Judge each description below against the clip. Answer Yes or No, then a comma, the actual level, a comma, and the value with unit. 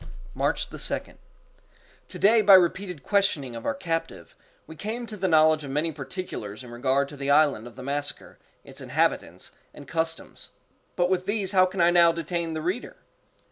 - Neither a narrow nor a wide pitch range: Yes, average, 4.7 semitones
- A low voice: No, medium, 165 Hz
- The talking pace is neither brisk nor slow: Yes, average, 175 wpm